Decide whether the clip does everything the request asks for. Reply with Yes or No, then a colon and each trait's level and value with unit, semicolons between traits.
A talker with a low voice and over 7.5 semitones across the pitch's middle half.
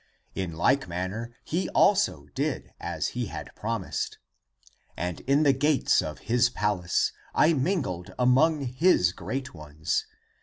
Yes: low, 120 Hz; wide, 8.0 semitones